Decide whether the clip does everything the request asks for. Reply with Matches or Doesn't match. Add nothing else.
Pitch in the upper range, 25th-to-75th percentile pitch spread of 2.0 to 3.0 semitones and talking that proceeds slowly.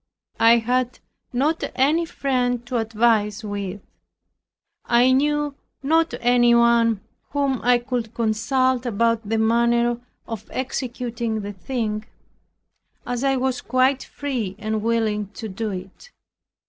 Matches